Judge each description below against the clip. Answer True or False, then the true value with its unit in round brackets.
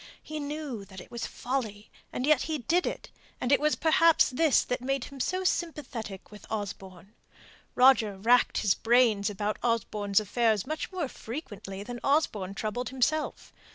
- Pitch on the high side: True (245 Hz)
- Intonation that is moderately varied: False (6.0 semitones)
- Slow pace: False (160 wpm)